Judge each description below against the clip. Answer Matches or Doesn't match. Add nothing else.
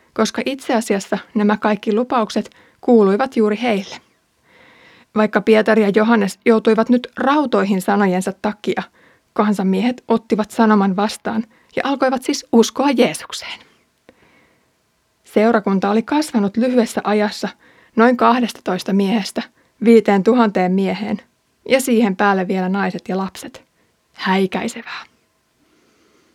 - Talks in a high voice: Matches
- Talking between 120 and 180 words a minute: Doesn't match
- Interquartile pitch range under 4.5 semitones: Matches